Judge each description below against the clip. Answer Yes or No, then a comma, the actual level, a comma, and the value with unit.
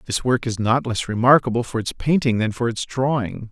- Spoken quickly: Yes, fast, 220 wpm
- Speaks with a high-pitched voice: No, low, 120 Hz